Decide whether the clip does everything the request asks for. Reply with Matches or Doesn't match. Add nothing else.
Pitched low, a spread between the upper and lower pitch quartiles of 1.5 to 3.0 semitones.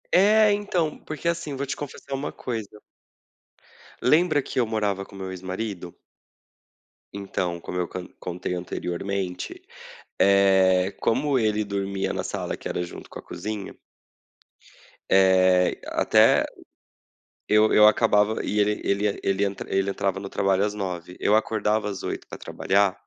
Matches